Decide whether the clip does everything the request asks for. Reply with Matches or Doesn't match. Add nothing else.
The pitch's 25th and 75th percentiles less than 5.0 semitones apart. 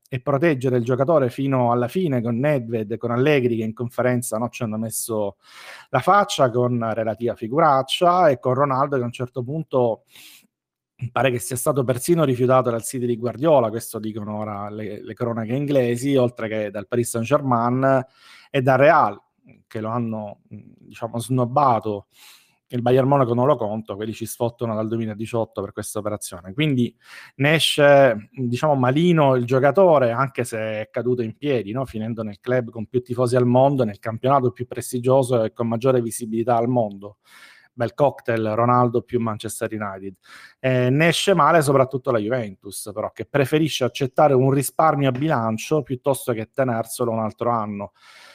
Matches